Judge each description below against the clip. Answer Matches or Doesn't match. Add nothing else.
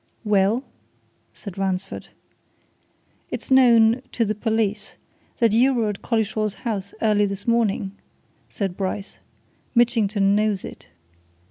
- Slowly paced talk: Matches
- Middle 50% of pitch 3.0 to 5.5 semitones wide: Doesn't match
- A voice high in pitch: Matches